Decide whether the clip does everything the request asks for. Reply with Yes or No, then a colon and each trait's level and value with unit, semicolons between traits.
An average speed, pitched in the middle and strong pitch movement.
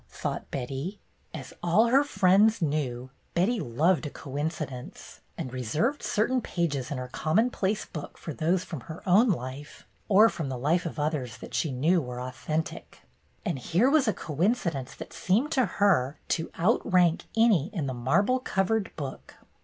Yes: average, 165 wpm; medium, 165 Hz; wide, 6.9 semitones